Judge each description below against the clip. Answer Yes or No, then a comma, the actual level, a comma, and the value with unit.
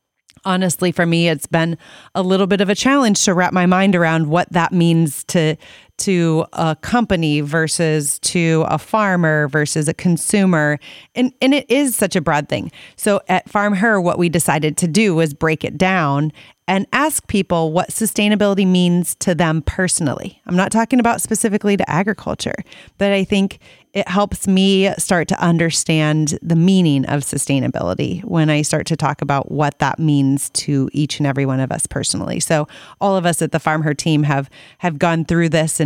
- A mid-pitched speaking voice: Yes, medium, 170 Hz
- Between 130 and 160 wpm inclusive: No, average, 185 wpm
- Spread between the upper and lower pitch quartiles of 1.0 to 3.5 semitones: No, average, 3.9 semitones